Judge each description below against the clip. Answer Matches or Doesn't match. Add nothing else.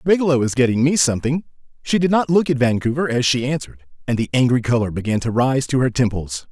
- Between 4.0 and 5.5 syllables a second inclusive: Doesn't match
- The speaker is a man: Matches